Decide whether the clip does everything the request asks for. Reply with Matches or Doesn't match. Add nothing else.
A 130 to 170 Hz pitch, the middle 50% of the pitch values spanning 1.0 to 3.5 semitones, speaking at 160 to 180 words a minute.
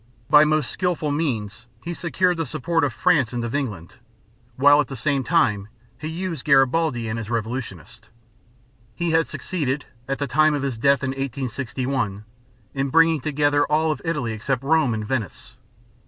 Doesn't match